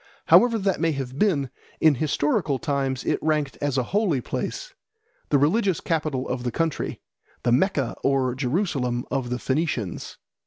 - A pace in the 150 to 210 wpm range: Yes, average, 155 wpm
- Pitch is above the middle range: No, medium, 140 Hz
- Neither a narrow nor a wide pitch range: Yes, average, 4.2 semitones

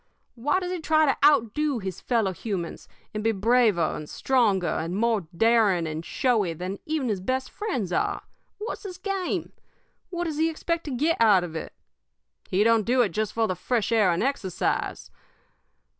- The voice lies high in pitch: Yes, high, 230 Hz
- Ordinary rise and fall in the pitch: No, wide, 7.5 semitones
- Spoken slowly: No, average, 180 wpm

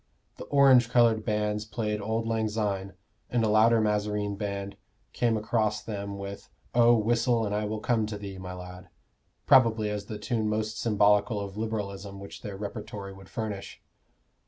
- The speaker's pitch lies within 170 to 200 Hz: No, low, 105 Hz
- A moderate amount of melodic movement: No, narrow, 1.9 semitones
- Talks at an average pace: Yes, average, 170 wpm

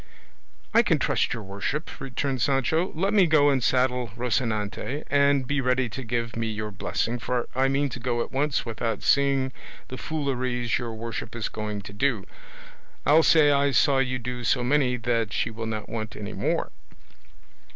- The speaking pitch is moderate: No, low, 125 Hz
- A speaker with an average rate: Yes, average, 180 wpm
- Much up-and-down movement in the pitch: No, average, 3.5 semitones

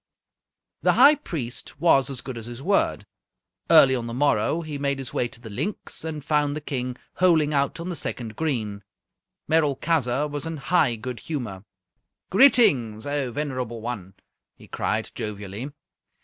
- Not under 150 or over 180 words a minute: Yes, average, 160 wpm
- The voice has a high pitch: No, low, 135 Hz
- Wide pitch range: No, average, 4.6 semitones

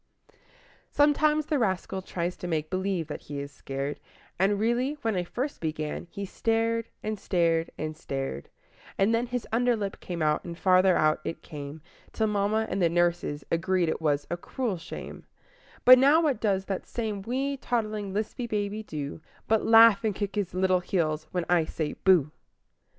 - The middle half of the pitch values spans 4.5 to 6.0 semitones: Yes, average, 5.2 semitones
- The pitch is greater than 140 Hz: Yes, high, 190 Hz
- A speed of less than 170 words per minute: No, average, 180 wpm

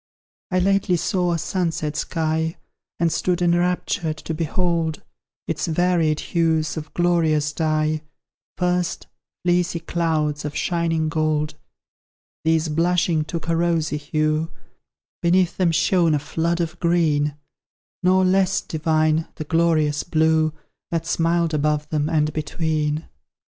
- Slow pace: Yes, slow, 125 wpm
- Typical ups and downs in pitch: No, narrow, 1.9 semitones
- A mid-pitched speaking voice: Yes, medium, 160 Hz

